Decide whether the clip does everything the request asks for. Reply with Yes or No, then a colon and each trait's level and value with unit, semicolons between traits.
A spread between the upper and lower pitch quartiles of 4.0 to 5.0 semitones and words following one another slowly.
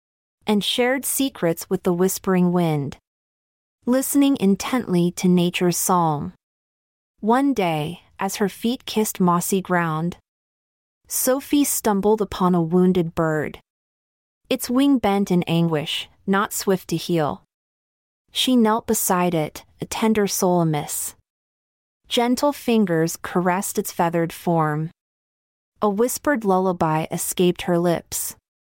Yes: average, 4.5 semitones; slow, 115 wpm